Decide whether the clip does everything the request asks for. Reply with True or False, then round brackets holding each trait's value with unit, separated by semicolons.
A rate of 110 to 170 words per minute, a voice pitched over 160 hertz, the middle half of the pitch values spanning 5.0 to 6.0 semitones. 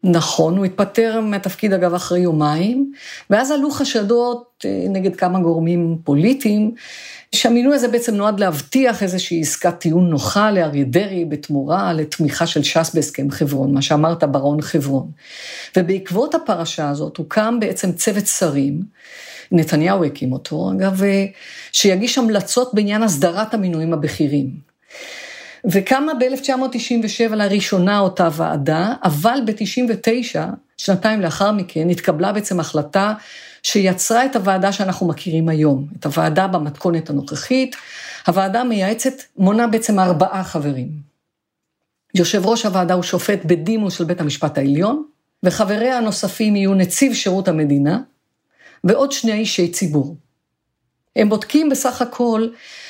True (120 wpm; 190 Hz; 5.4 semitones)